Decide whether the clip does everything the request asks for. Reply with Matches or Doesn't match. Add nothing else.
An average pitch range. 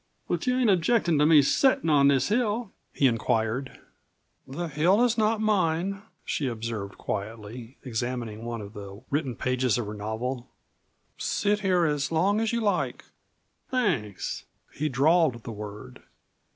Doesn't match